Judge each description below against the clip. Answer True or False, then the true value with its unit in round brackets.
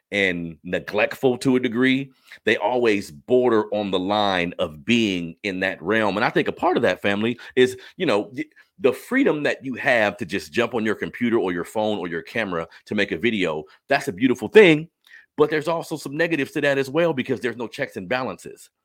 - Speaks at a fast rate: True (215 wpm)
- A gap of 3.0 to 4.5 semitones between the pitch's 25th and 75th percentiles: False (5.4 semitones)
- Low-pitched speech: True (125 Hz)